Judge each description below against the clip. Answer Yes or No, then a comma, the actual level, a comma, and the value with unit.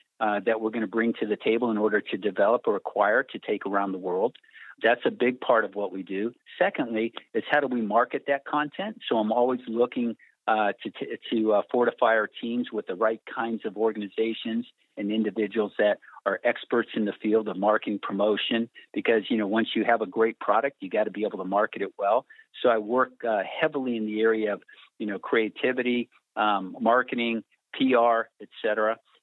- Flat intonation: Yes, narrow, 1.9 semitones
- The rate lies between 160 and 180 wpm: No, fast, 205 wpm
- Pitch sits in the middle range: No, low, 115 Hz